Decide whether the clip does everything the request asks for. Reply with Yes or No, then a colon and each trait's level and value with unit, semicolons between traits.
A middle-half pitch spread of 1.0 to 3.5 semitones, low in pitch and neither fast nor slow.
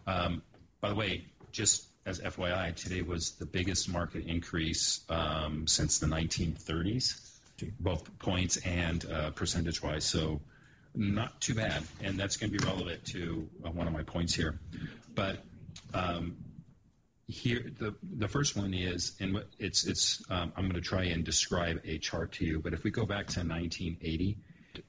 Yes: average, 2.9 semitones; very low, 85 Hz; average, 165 wpm